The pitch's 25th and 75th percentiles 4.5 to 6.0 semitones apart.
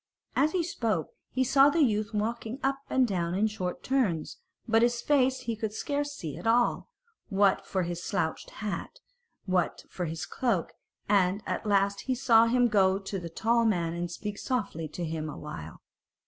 Yes: average, 5.3 semitones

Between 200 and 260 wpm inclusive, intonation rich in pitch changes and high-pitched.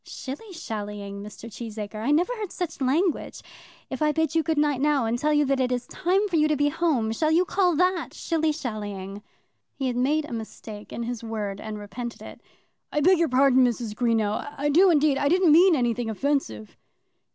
Yes: fast, 205 wpm; wide, 6.0 semitones; very high, 275 Hz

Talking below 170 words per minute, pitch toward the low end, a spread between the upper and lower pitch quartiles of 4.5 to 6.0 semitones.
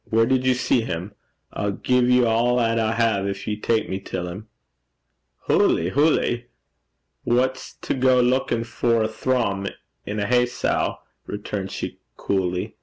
No: average, 160 wpm; low, 115 Hz; average, 3.5 semitones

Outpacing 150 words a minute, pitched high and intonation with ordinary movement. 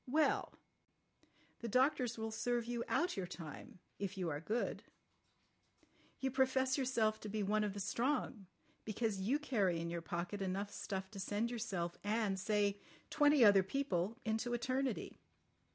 No: average, 145 wpm; high, 215 Hz; average, 4.2 semitones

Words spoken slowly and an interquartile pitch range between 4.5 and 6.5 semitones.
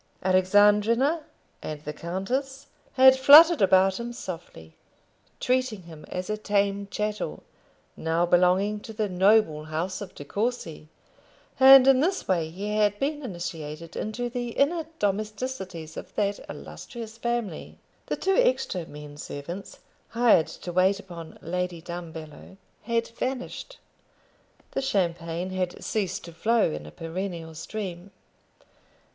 Yes: slow, 130 wpm; wide, 5.6 semitones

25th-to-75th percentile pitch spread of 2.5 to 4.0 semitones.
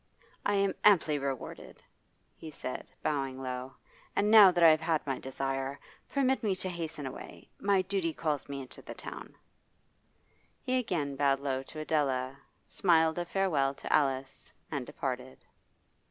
No: average, 5.0 semitones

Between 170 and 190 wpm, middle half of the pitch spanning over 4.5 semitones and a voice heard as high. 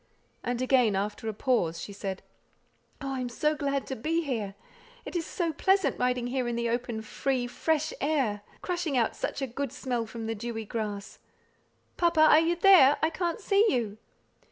Yes: average, 185 wpm; wide, 5.6 semitones; very high, 255 Hz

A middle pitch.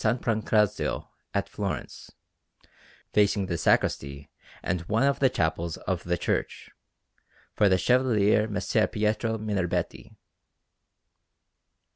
No: low, 105 Hz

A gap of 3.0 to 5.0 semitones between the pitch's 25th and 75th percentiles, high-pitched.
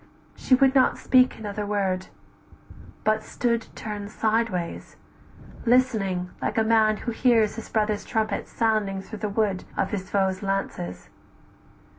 No: narrow, 2.5 semitones; high, 215 Hz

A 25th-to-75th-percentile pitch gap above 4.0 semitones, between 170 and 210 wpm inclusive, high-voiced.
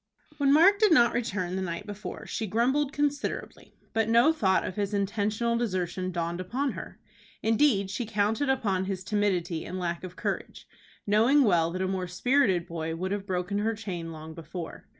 Yes: average, 4.5 semitones; average, 180 wpm; high, 200 Hz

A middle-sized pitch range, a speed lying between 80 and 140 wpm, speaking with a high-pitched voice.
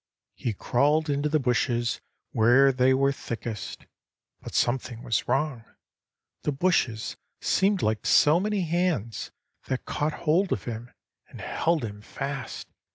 No: average, 4.6 semitones; slow, 135 wpm; low, 135 Hz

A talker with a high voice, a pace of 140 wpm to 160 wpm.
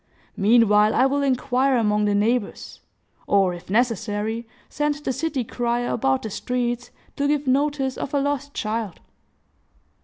Yes: high, 240 Hz; average, 145 wpm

